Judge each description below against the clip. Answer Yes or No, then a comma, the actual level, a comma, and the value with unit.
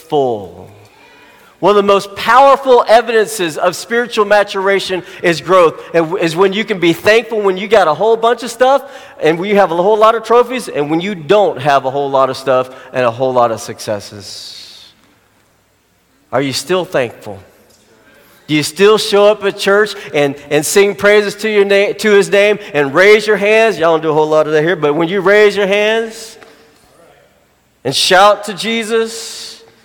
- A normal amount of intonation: No, wide, 6.7 semitones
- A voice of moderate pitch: No, high, 195 Hz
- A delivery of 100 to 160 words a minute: No, average, 190 wpm